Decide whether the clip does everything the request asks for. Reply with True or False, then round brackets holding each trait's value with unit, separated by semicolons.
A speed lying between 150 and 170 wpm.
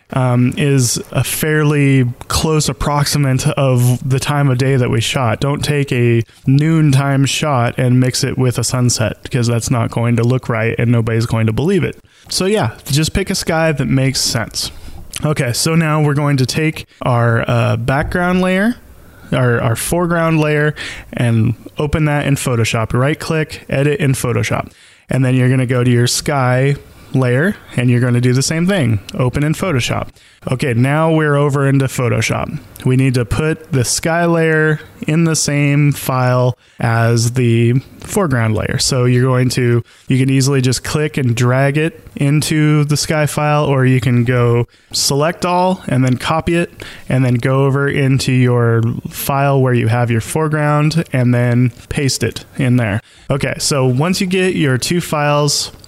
False (180 wpm)